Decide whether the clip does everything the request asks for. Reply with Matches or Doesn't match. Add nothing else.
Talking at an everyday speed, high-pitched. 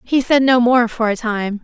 Doesn't match